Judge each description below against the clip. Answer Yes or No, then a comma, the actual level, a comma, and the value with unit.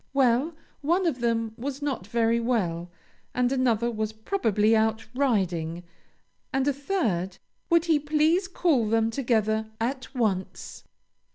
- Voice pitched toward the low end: No, high, 235 Hz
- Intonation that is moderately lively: Yes, average, 4.5 semitones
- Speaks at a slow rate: Yes, slow, 130 wpm